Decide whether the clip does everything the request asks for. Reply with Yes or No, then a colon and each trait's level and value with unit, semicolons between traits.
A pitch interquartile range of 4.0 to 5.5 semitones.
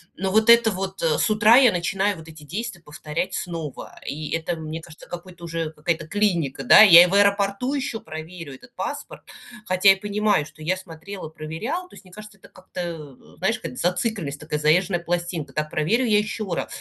Yes: average, 4.4 semitones